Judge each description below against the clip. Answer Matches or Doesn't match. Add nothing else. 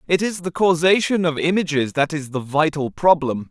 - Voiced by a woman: Doesn't match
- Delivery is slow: Doesn't match